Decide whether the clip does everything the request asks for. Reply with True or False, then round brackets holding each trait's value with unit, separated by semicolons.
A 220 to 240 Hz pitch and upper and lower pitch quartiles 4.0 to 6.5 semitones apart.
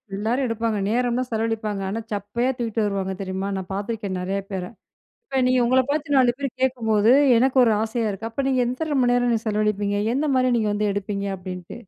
False (225 Hz; 3.5 semitones)